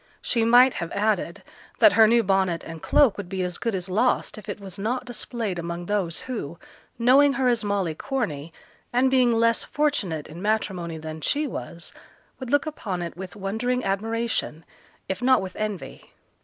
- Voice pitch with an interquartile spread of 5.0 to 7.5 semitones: Yes, wide, 5.5 semitones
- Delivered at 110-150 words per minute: No, average, 180 wpm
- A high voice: Yes, high, 210 Hz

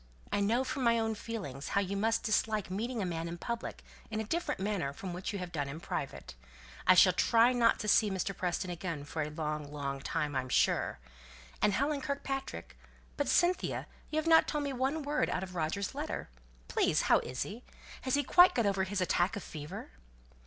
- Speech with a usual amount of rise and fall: No, wide, 6.2 semitones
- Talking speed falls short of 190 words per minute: No, average, 195 wpm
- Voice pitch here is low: No, high, 200 Hz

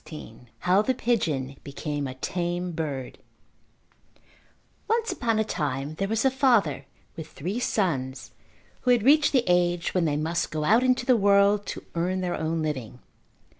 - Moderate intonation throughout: No, wide, 6.6 semitones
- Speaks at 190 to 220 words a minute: No, average, 165 wpm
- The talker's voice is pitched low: No, medium, 175 Hz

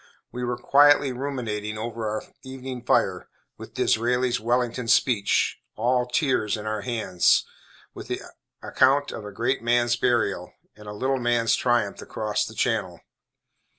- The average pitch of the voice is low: Yes, low, 120 Hz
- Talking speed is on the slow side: No, average, 145 wpm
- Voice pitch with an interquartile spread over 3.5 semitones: No, average, 2.7 semitones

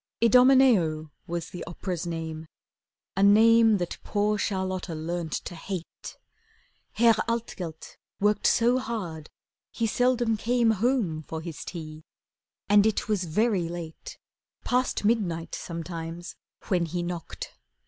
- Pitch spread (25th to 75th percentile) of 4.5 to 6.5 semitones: Yes, wide, 5.4 semitones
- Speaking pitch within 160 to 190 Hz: Yes, medium, 185 Hz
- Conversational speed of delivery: No, slow, 120 wpm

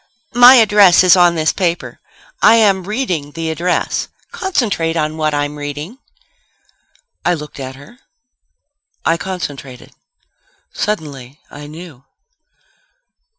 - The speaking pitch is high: No, medium, 165 Hz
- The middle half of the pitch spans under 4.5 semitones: No, average, 5.2 semitones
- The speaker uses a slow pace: Yes, slow, 110 wpm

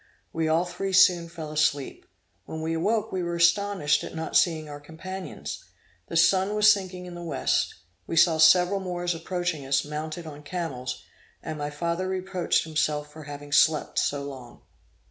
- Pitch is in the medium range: Yes, medium, 165 Hz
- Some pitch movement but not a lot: Yes, average, 3.2 semitones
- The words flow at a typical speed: Yes, average, 170 wpm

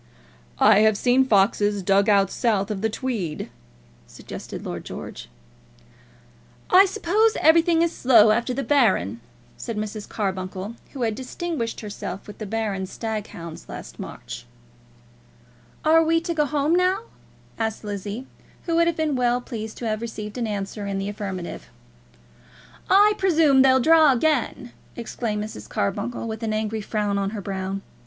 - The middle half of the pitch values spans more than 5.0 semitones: Yes, wide, 5.5 semitones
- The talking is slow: No, average, 155 wpm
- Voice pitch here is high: Yes, high, 220 Hz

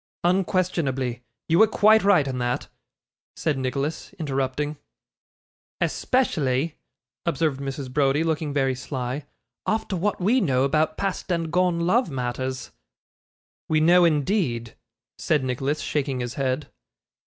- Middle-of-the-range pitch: Yes, medium, 150 Hz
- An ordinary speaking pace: No, slow, 120 wpm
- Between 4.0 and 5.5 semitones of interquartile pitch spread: Yes, average, 4.8 semitones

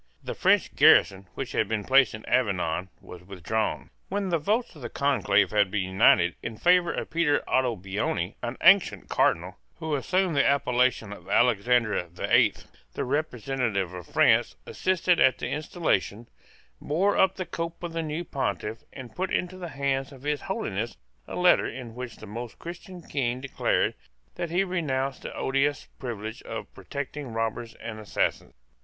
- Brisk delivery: No, average, 165 wpm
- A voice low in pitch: Yes, low, 130 Hz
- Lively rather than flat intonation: Yes, wide, 7.1 semitones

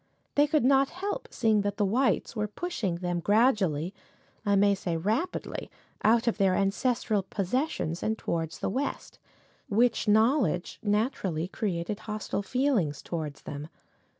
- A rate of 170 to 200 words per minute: No, average, 145 wpm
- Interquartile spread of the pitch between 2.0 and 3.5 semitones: No, average, 5.2 semitones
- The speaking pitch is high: Yes, high, 210 Hz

